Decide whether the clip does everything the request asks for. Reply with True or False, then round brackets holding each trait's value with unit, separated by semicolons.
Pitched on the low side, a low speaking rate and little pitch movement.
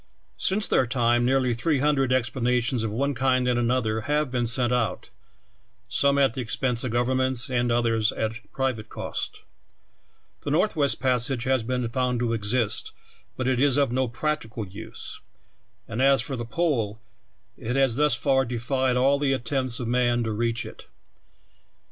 False (125 Hz; 165 wpm; 2.2 semitones)